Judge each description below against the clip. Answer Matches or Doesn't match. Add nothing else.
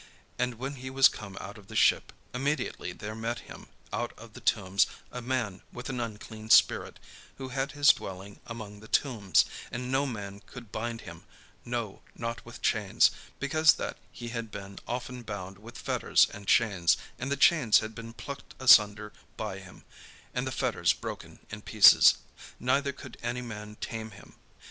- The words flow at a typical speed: Matches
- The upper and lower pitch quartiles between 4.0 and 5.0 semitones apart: Doesn't match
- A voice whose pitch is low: Matches